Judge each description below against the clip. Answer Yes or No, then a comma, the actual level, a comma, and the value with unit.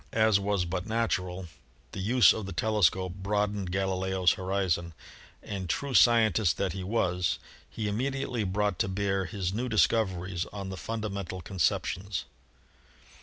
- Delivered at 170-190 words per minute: No, average, 150 wpm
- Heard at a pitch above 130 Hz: No, very low, 95 Hz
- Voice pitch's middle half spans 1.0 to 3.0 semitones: Yes, narrow, 2.4 semitones